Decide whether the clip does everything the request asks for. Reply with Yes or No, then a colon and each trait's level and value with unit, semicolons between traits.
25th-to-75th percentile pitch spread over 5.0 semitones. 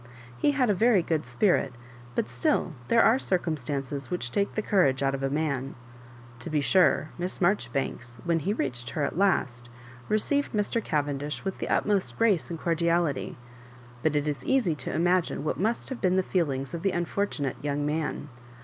Yes: wide, 5.6 semitones